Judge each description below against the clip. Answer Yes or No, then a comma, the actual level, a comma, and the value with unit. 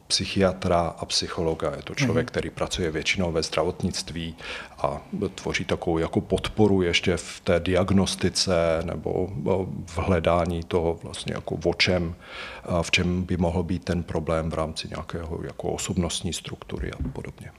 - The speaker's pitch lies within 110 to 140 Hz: No, very low, 90 Hz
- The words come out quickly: No, average, 145 wpm